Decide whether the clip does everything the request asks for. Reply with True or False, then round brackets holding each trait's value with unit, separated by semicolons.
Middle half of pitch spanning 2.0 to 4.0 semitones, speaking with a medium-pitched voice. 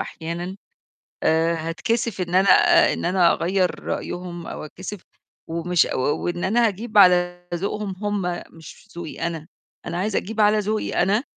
True (3.4 semitones; 180 Hz)